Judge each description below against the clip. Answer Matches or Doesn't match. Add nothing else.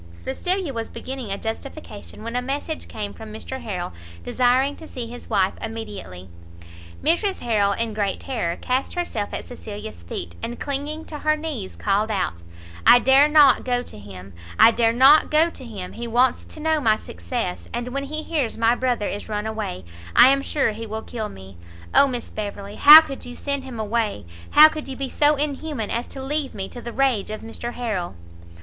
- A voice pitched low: Doesn't match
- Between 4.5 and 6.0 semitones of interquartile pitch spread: Matches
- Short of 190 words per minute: Doesn't match